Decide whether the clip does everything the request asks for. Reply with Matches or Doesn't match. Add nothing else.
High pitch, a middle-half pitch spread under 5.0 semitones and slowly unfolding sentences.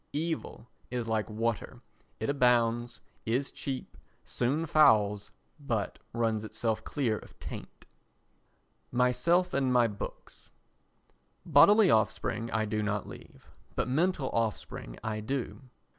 Doesn't match